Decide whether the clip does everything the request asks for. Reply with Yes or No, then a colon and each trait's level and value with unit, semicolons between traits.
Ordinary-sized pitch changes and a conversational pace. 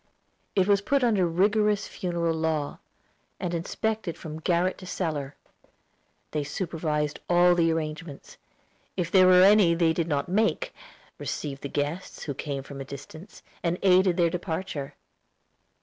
Yes: average, 3.5 semitones; average, 150 wpm